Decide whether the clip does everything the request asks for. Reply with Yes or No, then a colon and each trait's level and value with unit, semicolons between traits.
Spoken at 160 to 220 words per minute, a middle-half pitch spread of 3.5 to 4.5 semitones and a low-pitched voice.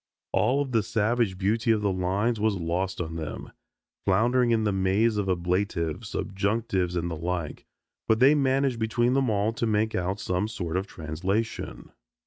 Yes: average, 170 wpm; average, 3.9 semitones; low, 105 Hz